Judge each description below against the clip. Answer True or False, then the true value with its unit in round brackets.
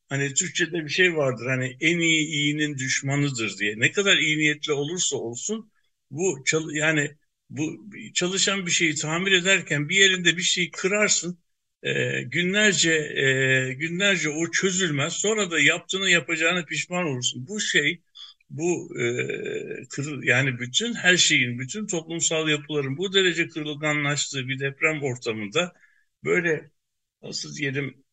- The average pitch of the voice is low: False (160 Hz)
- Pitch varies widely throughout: False (4.2 semitones)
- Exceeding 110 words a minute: True (135 wpm)